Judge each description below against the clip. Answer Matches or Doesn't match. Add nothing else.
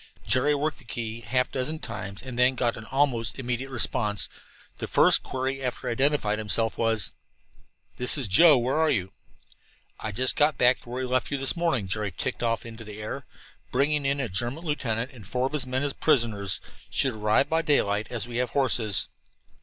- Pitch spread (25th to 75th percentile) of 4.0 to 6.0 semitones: Doesn't match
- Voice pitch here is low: Matches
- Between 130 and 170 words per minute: Doesn't match